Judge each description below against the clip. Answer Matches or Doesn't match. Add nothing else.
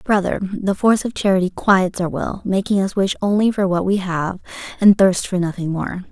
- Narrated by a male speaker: Doesn't match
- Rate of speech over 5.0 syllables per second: Matches